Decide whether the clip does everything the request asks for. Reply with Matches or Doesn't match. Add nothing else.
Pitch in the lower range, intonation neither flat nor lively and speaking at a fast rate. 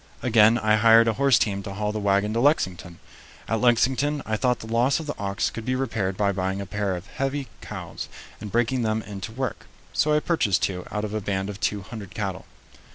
Matches